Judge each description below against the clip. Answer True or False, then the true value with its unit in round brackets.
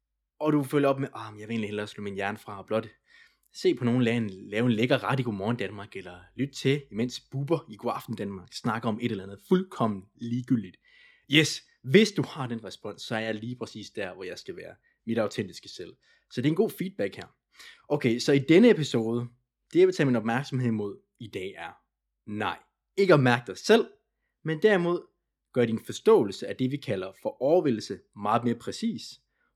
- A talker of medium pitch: False (120 Hz)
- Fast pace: False (215 wpm)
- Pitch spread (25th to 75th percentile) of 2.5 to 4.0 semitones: False (5.0 semitones)